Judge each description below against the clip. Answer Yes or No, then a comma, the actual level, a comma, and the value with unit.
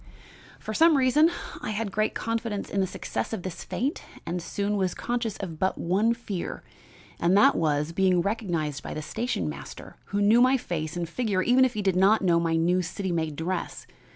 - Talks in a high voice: Yes, high, 195 Hz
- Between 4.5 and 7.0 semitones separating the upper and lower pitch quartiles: Yes, average, 4.8 semitones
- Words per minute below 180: No, average, 200 wpm